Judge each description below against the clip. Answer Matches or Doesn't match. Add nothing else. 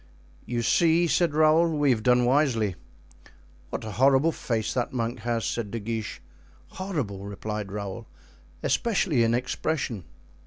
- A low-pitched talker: Matches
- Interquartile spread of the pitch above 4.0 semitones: Matches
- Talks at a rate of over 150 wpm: Doesn't match